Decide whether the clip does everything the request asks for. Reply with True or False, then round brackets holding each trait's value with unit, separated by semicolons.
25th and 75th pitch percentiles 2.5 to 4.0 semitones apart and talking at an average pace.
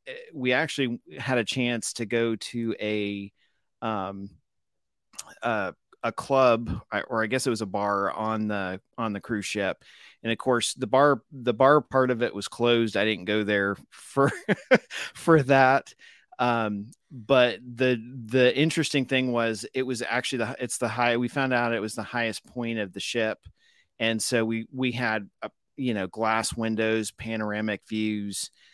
True (2.9 semitones; 170 wpm)